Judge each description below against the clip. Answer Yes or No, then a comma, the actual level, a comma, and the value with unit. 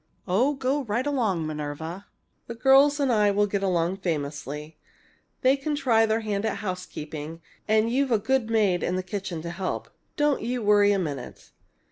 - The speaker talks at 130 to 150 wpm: No, average, 175 wpm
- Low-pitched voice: No, high, 205 Hz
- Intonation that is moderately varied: No, wide, 6.3 semitones